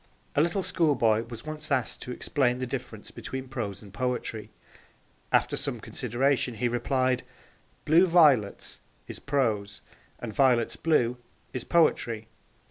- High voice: No, low, 125 Hz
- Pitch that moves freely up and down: No, average, 3.7 semitones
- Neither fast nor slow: No, slow, 130 wpm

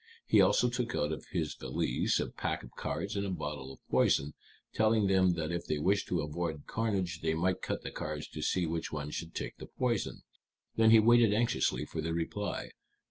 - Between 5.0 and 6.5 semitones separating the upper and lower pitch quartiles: Yes, wide, 5.4 semitones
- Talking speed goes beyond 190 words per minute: Yes, fast, 205 wpm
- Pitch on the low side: Yes, very low, 85 Hz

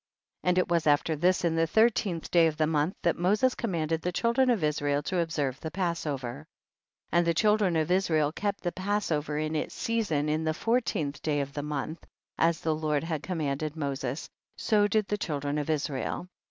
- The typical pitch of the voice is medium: Yes, medium, 160 Hz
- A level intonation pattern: No, average, 3.6 semitones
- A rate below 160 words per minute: No, fast, 205 wpm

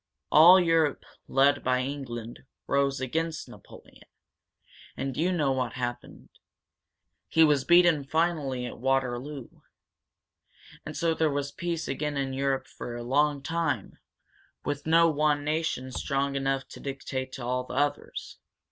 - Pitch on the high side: No, medium, 140 Hz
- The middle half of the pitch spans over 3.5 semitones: No, average, 3.1 semitones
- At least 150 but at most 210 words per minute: No, average, 140 wpm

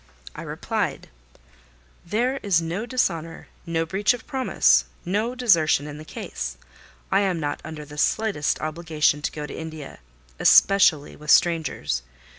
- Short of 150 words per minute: Yes, average, 140 wpm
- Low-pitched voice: No, medium, 165 Hz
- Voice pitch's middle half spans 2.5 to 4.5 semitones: No, average, 5.0 semitones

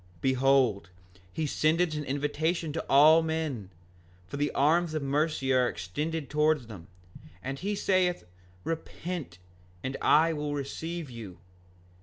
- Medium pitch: Yes, medium, 150 Hz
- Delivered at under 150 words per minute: Yes, slow, 135 wpm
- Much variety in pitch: No, average, 3.3 semitones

